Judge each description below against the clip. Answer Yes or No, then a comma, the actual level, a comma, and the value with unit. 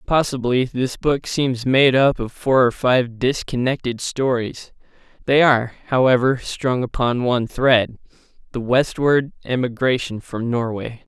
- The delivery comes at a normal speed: No, slow, 125 wpm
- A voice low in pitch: Yes, low, 125 Hz